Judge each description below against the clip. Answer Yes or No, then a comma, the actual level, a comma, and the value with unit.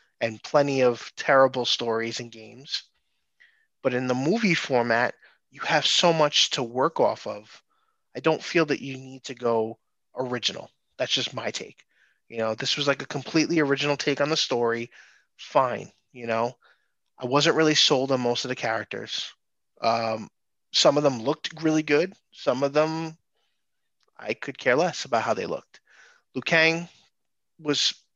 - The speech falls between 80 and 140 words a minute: No, average, 165 wpm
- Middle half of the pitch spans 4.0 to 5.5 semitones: Yes, average, 4.4 semitones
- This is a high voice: No, low, 135 Hz